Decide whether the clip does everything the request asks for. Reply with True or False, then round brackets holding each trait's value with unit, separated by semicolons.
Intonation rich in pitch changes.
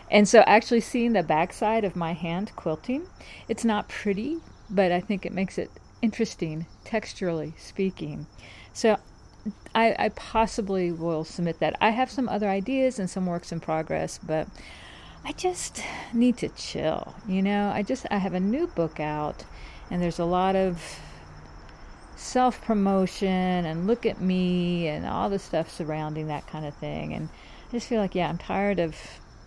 False (4.8 semitones)